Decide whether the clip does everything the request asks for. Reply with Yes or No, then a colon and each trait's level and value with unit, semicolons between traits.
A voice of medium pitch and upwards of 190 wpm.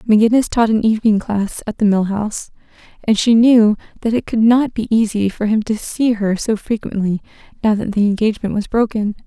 No: high, 215 Hz; average, 200 wpm